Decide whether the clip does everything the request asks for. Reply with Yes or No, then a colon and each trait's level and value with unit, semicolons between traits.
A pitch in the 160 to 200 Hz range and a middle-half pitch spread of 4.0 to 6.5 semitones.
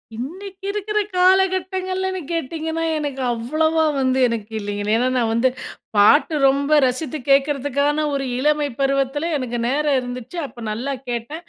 No: very high, 285 Hz; average, 4.6 semitones